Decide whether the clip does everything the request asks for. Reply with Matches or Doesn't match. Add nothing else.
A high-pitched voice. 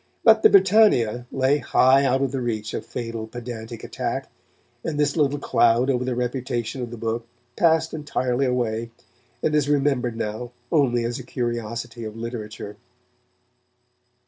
Doesn't match